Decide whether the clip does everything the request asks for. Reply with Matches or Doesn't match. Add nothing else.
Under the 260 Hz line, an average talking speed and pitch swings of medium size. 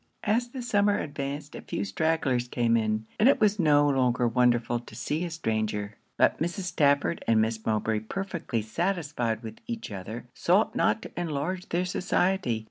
Doesn't match